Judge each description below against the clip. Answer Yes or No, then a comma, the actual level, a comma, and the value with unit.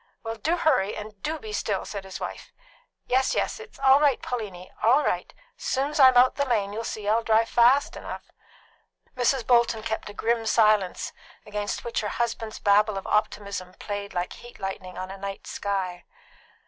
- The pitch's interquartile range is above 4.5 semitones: No, average, 3.5 semitones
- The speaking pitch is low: No, high, 220 Hz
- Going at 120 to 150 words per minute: No, average, 180 wpm